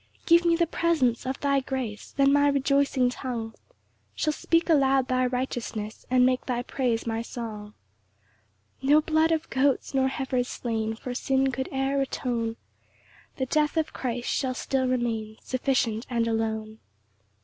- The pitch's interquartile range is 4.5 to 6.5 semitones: No, average, 3.0 semitones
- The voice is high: Yes, very high, 255 Hz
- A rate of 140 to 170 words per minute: Yes, average, 160 wpm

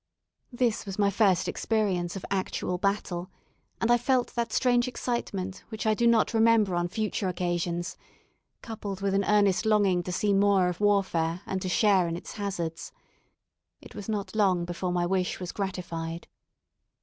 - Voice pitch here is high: Yes, high, 195 Hz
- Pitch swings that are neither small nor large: Yes, average, 3.3 semitones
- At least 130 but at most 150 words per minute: No, average, 165 wpm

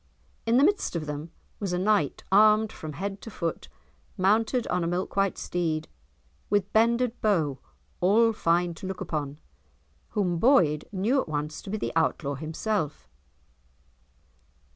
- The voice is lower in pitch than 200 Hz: Yes, high, 190 Hz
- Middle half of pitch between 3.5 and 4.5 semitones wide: No, average, 5.2 semitones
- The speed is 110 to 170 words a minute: Yes, average, 150 wpm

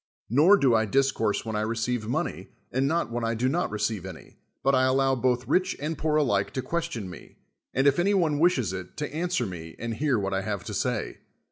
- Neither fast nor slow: No, fast, 235 wpm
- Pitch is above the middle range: No, low, 125 Hz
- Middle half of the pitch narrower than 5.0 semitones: No, wide, 5.5 semitones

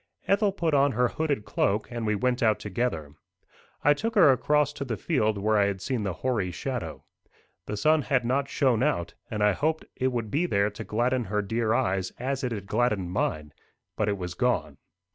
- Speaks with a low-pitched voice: Yes, low, 115 Hz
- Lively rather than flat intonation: No, average, 5.0 semitones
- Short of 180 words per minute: No, fast, 205 wpm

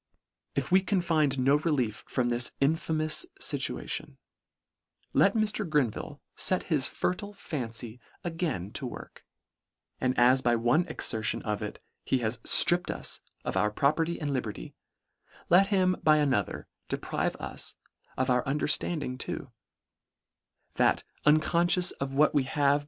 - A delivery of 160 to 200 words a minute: No, average, 145 wpm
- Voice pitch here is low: No, medium, 145 Hz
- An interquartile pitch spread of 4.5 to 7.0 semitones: Yes, average, 5.2 semitones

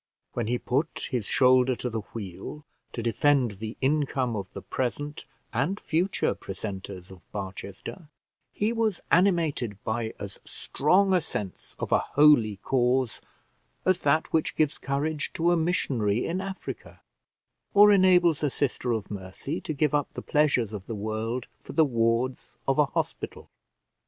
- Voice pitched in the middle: No, low, 130 Hz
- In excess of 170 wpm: No, average, 155 wpm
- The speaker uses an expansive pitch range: Yes, wide, 5.9 semitones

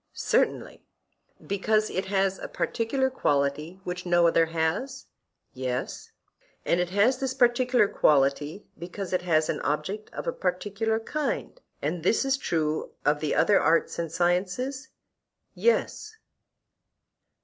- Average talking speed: No, slow, 130 wpm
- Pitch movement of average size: No, wide, 6.4 semitones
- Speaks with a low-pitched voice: No, medium, 185 Hz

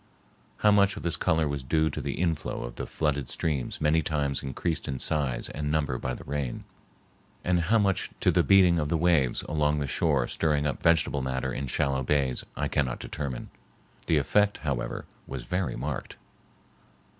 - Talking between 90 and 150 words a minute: No, average, 180 wpm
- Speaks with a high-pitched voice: No, very low, 75 Hz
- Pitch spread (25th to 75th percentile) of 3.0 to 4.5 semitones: Yes, average, 3.5 semitones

